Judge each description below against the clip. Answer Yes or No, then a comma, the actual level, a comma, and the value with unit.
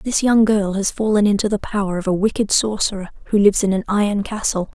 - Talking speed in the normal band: No, fast, 225 wpm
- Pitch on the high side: Yes, high, 205 Hz